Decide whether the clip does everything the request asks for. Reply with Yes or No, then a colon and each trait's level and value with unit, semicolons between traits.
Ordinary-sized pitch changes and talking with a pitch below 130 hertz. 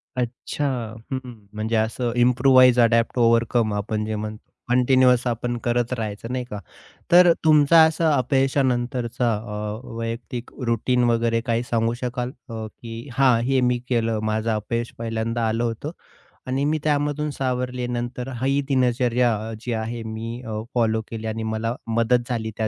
No: narrow, 2.0 semitones; low, 120 Hz